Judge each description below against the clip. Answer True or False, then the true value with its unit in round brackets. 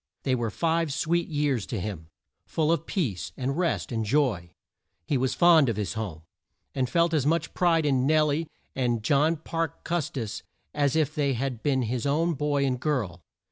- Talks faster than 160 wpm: True (190 wpm)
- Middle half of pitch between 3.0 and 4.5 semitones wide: False (5.0 semitones)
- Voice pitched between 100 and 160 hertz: True (140 Hz)